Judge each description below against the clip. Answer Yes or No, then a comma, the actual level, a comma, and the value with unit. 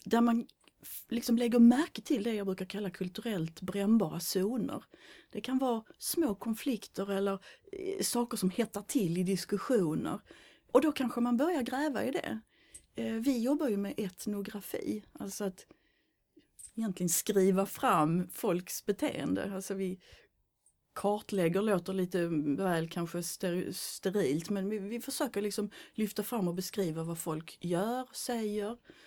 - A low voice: No, high, 205 Hz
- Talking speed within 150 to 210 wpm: No, average, 140 wpm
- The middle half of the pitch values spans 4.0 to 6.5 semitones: Yes, average, 4.3 semitones